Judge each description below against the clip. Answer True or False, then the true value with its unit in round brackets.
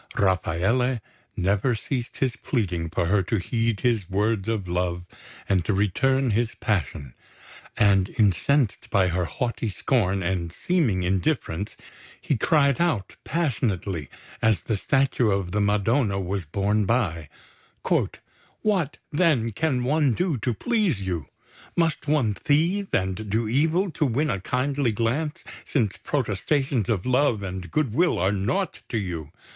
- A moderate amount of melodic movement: False (6.2 semitones)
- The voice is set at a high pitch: False (110 Hz)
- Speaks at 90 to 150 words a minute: True (140 wpm)